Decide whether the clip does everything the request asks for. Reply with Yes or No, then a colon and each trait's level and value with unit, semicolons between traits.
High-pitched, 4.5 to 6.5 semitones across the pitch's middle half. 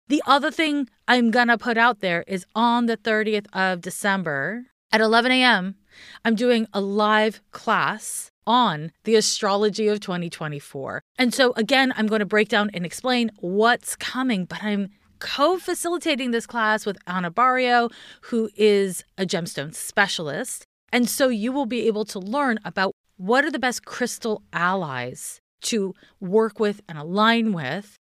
No: high, 215 Hz; average, 4.1 semitones